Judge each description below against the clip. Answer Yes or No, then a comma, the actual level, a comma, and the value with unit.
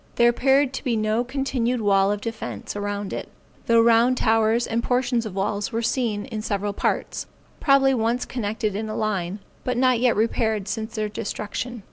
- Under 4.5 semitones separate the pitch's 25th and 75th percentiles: Yes, average, 2.9 semitones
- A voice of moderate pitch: No, high, 225 Hz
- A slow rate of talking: No, average, 175 wpm